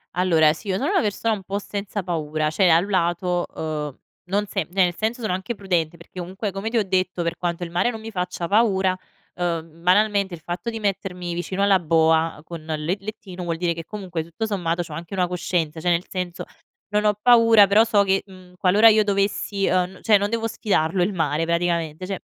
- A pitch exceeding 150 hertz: Yes, medium, 185 Hz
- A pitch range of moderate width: Yes, average, 3.2 semitones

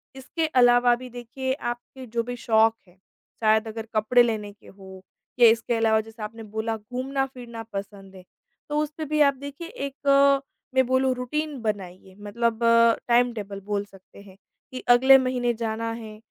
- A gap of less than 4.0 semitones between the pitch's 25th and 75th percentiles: Yes, average, 3.2 semitones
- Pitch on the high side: Yes, high, 235 Hz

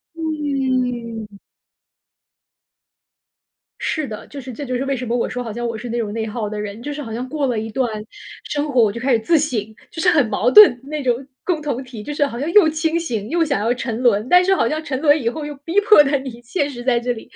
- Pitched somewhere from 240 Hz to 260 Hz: Yes, very high, 255 Hz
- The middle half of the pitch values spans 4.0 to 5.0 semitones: Yes, average, 4.4 semitones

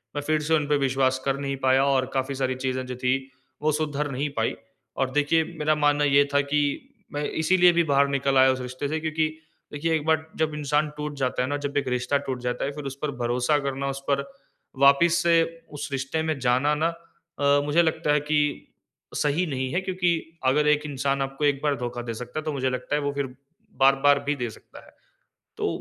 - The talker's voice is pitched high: No, medium, 140 Hz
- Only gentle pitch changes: Yes, narrow, 2.2 semitones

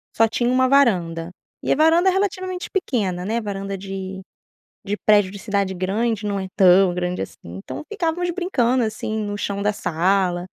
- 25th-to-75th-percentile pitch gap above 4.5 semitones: Yes, wide, 5.4 semitones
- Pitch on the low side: No, high, 205 Hz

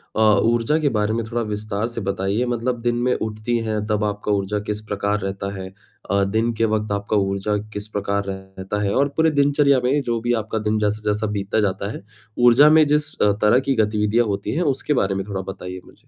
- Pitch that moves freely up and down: No, average, 2.9 semitones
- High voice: No, low, 105 Hz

